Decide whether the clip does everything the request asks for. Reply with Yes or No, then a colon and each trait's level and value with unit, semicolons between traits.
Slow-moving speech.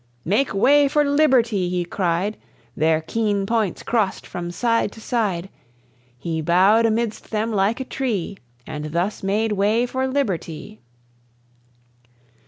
Yes: slow, 130 wpm